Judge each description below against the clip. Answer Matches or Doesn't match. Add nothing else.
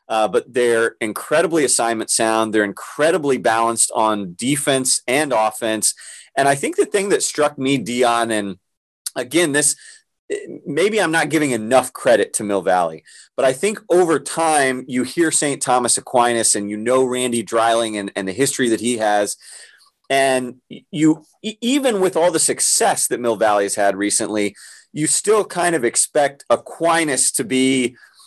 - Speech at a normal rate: Matches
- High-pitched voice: Doesn't match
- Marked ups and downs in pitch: Matches